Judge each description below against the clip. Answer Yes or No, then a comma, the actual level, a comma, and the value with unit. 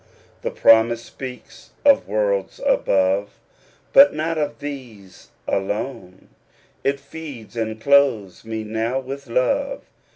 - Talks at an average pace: No, slow, 110 wpm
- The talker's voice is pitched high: No, low, 115 Hz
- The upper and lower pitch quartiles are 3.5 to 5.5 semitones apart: Yes, average, 5.0 semitones